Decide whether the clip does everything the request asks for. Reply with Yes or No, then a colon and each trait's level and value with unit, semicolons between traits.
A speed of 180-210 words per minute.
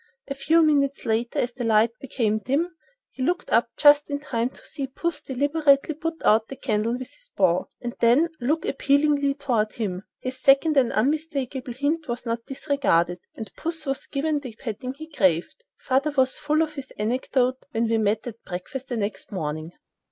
Yes: average, 185 wpm